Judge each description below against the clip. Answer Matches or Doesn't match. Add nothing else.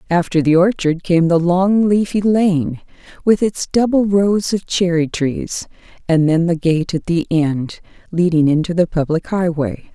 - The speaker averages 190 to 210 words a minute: Doesn't match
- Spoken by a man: Doesn't match